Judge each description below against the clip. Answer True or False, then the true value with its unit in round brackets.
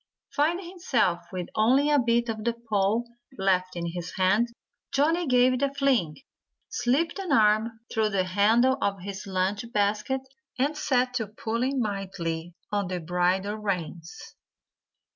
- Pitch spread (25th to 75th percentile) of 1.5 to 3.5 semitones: False (5.3 semitones)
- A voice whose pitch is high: True (215 Hz)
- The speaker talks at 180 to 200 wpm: False (145 wpm)